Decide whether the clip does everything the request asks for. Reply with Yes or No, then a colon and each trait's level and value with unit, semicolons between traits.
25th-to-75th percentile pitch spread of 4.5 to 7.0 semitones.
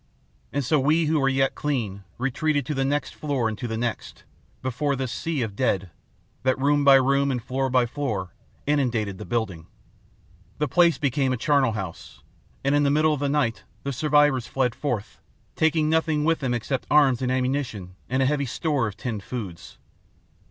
No: average, 3.5 semitones